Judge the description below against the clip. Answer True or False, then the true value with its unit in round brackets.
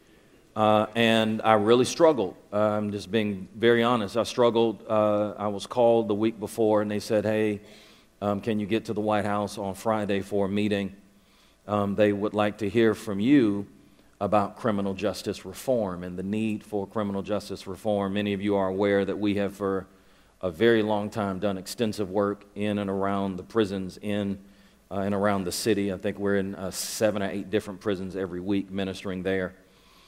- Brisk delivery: False (195 wpm)